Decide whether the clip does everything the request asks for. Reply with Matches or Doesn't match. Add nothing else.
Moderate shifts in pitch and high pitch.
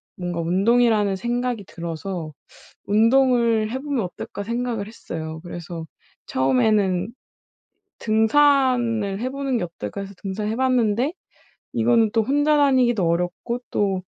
Matches